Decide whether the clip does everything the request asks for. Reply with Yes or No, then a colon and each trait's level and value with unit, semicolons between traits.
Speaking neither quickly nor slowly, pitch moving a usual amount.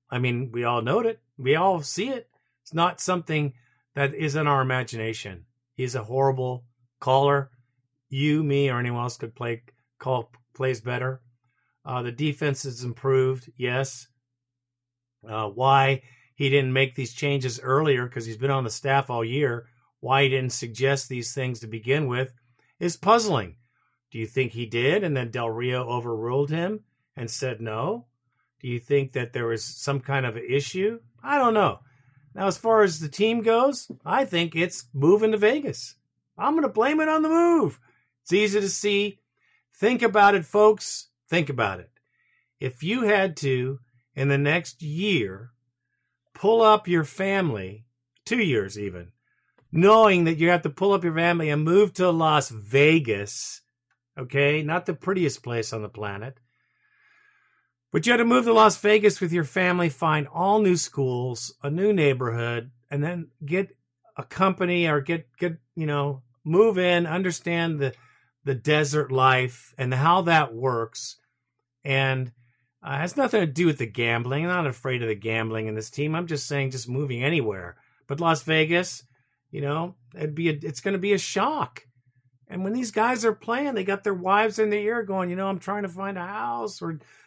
No: average, 180 wpm; wide, 6.3 semitones